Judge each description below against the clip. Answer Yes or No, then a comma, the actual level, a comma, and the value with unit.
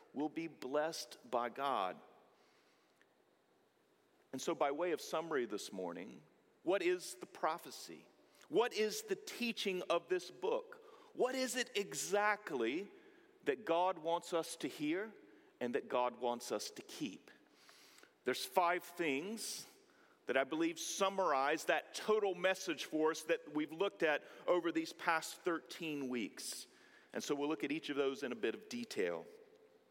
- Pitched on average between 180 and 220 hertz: Yes, high, 190 Hz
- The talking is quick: No, average, 150 wpm